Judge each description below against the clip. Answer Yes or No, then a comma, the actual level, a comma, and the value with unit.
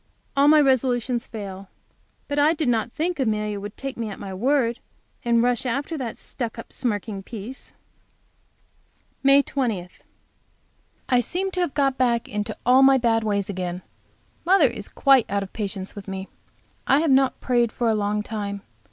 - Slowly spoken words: No, average, 170 wpm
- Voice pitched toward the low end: No, high, 235 Hz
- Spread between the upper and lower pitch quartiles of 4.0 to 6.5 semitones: Yes, average, 4.7 semitones